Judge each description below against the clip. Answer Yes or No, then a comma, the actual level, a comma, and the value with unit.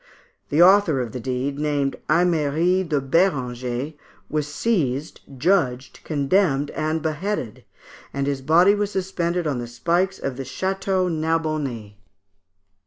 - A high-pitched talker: No, medium, 155 Hz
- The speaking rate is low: Yes, slow, 125 wpm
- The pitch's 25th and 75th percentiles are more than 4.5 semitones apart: Yes, average, 4.9 semitones